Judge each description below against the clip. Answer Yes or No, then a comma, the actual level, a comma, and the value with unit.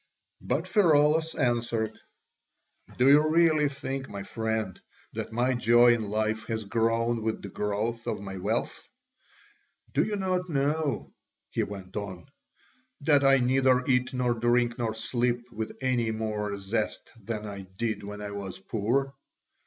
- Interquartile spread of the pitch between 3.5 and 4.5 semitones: Yes, average, 3.8 semitones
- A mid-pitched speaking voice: No, low, 115 Hz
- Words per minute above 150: No, average, 145 wpm